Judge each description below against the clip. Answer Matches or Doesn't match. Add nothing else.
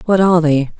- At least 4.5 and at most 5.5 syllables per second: Doesn't match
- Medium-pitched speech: Matches